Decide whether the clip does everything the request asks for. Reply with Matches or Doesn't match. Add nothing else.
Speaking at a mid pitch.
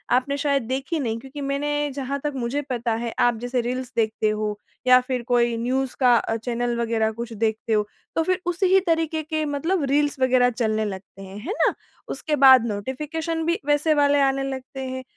Doesn't match